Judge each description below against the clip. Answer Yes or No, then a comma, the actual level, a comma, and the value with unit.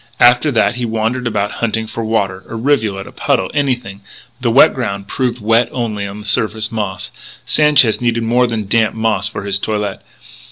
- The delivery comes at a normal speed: Yes, average, 190 wpm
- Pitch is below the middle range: Yes, low, 110 Hz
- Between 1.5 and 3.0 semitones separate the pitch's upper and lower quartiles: Yes, narrow, 2.6 semitones